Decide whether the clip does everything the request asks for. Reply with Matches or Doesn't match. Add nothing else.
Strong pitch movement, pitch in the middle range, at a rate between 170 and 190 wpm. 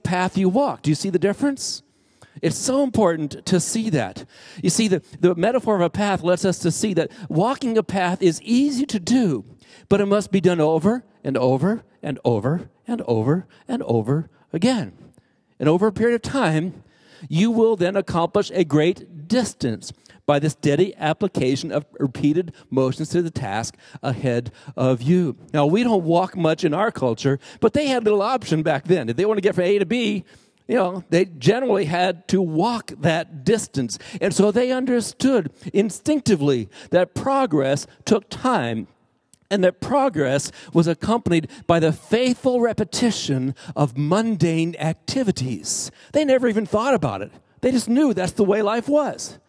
Matches